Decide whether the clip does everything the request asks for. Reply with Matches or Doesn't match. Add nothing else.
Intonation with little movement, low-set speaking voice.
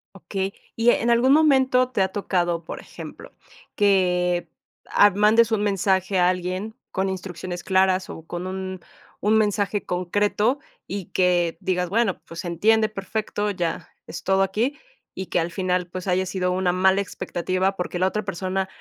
Doesn't match